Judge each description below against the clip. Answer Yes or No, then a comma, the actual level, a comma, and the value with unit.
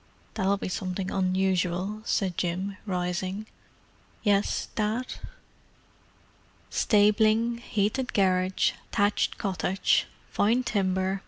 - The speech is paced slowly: Yes, slow, 85 wpm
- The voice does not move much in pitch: Yes, narrow, 2.3 semitones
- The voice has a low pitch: No, high, 195 Hz